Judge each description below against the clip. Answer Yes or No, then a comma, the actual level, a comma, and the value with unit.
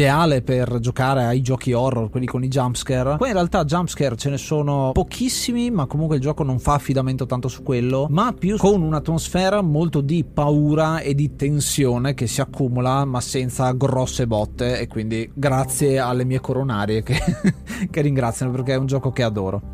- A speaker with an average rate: No, fast, 180 wpm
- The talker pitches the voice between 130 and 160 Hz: Yes, low, 135 Hz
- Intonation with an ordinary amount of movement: Yes, average, 3.2 semitones